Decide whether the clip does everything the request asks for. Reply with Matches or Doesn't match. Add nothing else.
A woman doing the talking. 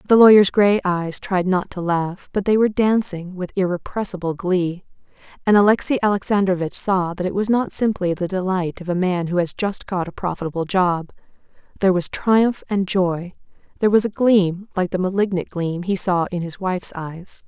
Matches